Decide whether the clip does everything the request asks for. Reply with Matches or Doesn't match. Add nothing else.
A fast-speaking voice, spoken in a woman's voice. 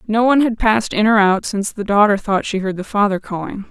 Matches